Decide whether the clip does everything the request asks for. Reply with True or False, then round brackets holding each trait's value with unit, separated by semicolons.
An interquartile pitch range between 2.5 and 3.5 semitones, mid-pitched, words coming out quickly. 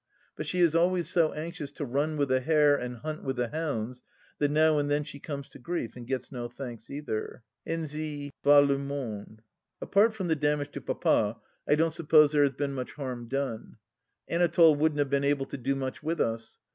True (2.9 semitones; 145 Hz; 210 wpm)